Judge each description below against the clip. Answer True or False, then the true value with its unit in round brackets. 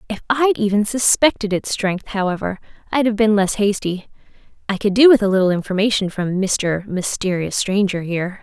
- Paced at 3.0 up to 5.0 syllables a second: False (5.3 syllables/s)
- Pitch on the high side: True (205 Hz)